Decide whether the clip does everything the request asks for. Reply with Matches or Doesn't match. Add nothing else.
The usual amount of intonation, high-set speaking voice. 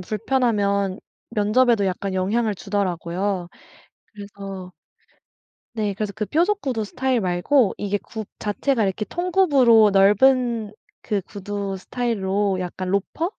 Matches